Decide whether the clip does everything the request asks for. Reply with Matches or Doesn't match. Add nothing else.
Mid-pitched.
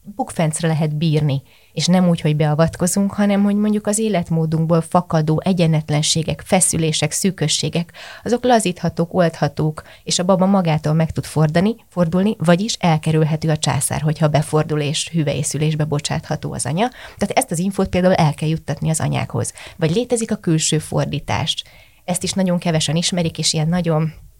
Matches